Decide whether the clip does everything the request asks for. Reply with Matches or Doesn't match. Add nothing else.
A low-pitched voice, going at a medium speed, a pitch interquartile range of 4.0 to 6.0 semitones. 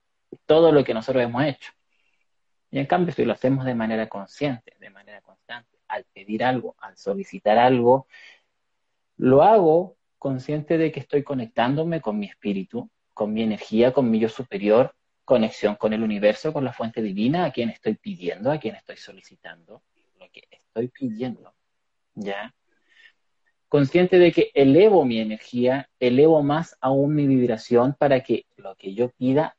Matches